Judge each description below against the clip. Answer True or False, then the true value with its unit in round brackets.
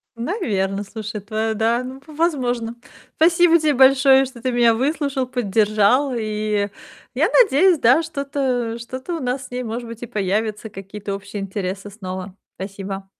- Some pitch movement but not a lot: True (4.5 semitones)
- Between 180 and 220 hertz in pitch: False (230 Hz)